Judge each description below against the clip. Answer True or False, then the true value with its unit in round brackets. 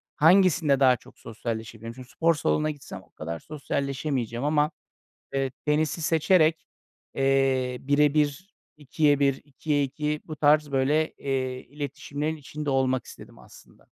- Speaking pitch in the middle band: True (145 Hz)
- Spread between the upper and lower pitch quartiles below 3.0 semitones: True (2.5 semitones)